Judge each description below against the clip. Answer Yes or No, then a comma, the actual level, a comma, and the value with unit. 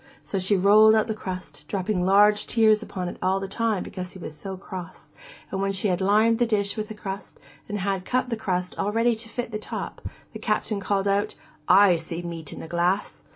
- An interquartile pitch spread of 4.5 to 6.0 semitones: No, average, 2.7 semitones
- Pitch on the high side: Yes, high, 200 Hz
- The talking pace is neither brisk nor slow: No, fast, 225 wpm